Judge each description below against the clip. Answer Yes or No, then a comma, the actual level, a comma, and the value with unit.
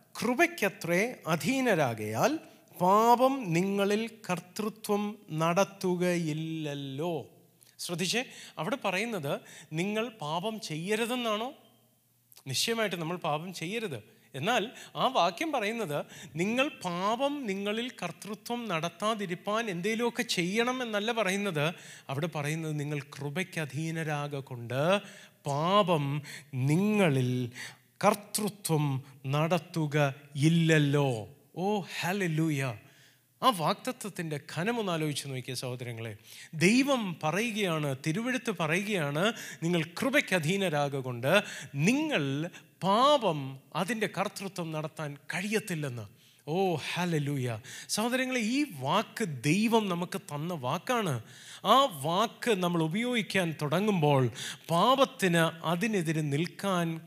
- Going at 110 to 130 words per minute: No, average, 80 wpm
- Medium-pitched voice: Yes, medium, 175 Hz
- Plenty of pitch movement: Yes, wide, 6.1 semitones